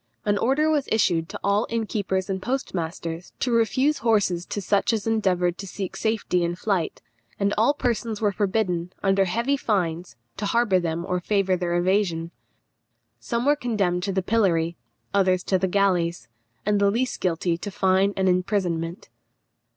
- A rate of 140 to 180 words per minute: Yes, average, 165 wpm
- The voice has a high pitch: Yes, high, 195 Hz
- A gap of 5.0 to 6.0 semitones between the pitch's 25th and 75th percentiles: No, average, 3.7 semitones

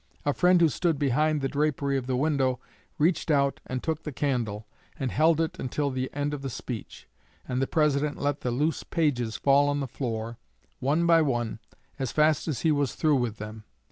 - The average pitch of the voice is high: No, medium, 140 Hz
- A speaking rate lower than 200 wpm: No, fast, 205 wpm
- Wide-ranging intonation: No, average, 3.2 semitones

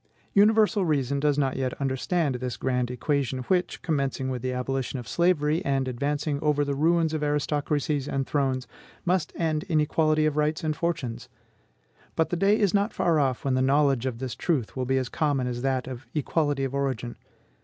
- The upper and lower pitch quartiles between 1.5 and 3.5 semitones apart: Yes, average, 3.1 semitones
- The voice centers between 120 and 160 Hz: Yes, medium, 140 Hz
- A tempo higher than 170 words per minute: Yes, average, 190 wpm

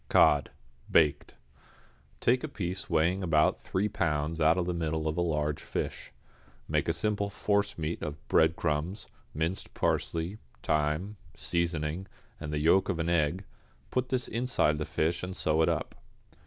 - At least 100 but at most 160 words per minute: Yes, average, 155 wpm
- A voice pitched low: Yes, very low, 85 Hz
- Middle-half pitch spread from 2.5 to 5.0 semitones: Yes, average, 3.8 semitones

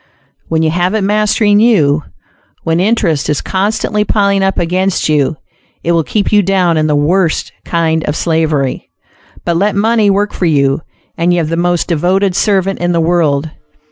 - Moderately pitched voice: Yes, medium, 175 Hz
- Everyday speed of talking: Yes, average, 175 wpm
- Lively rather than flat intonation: No, average, 3.7 semitones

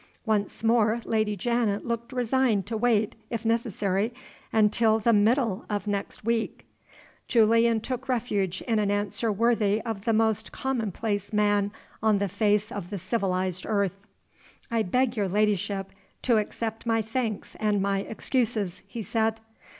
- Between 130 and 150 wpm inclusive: Yes, average, 145 wpm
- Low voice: No, high, 215 Hz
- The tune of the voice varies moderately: No, narrow, 2.2 semitones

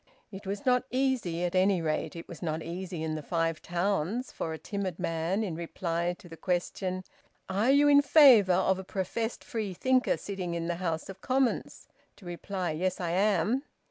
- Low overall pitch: No, medium, 185 Hz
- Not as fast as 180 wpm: No, average, 185 wpm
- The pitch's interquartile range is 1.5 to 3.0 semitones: No, average, 3.7 semitones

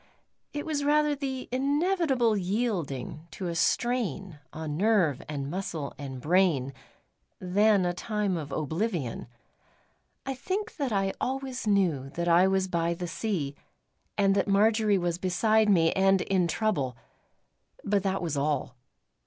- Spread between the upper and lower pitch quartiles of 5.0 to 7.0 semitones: Yes, average, 5.3 semitones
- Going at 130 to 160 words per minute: Yes, average, 140 wpm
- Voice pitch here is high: Yes, high, 195 Hz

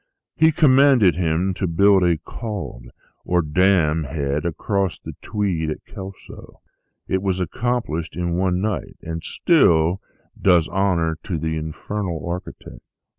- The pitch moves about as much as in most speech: Yes, average, 3.5 semitones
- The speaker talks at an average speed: No, slow, 130 wpm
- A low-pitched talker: Yes, very low, 90 Hz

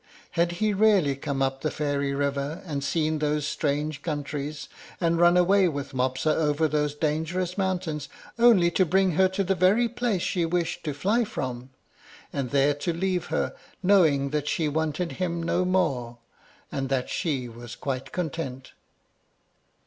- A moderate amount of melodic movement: Yes, average, 4.3 semitones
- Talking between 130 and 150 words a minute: No, average, 160 wpm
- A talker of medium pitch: Yes, medium, 155 Hz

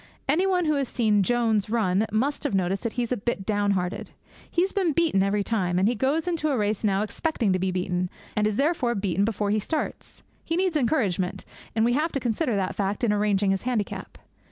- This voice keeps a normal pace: No, fast, 215 wpm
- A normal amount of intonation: No, wide, 5.8 semitones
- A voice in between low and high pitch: No, high, 220 Hz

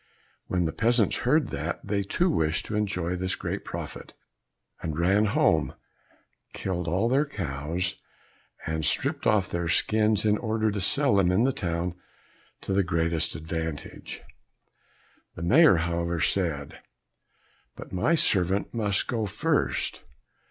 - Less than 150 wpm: Yes, average, 140 wpm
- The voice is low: Yes, very low, 95 Hz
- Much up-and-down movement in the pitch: No, average, 4.3 semitones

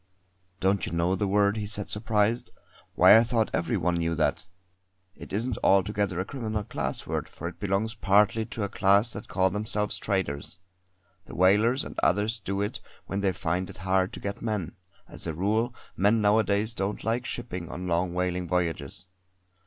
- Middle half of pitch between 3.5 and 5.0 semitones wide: No, average, 2.9 semitones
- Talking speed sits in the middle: Yes, average, 180 wpm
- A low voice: Yes, low, 100 Hz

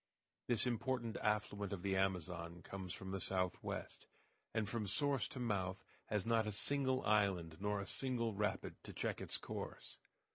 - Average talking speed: Yes, average, 160 wpm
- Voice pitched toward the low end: Yes, low, 105 Hz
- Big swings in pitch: No, average, 3.5 semitones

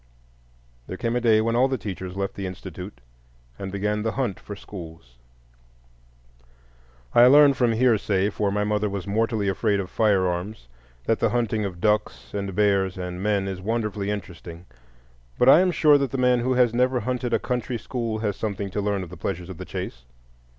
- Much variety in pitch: No, average, 3.7 semitones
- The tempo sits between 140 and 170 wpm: No, average, 190 wpm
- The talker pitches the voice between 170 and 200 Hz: No, low, 105 Hz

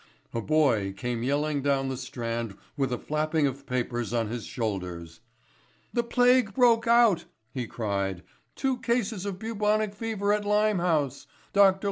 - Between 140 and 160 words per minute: Yes, average, 145 wpm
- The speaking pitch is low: No, medium, 150 Hz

